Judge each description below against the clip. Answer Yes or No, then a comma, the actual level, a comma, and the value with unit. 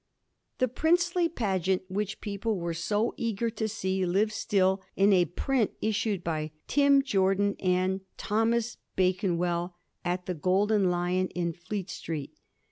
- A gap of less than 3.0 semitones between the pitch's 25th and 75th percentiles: No, average, 3.4 semitones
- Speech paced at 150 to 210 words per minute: No, average, 140 wpm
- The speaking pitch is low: No, high, 195 Hz